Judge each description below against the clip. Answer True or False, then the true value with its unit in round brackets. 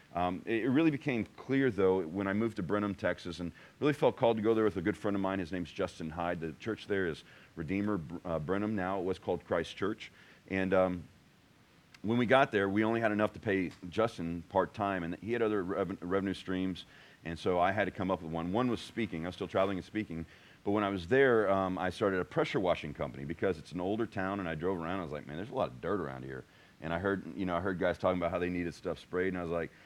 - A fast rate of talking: True (265 wpm)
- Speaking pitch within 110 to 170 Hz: False (95 Hz)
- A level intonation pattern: False (3.0 semitones)